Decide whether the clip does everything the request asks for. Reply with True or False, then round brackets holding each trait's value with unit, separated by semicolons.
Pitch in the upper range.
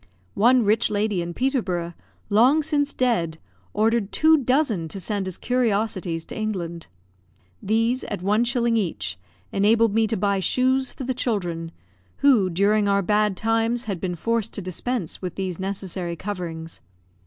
True (210 Hz)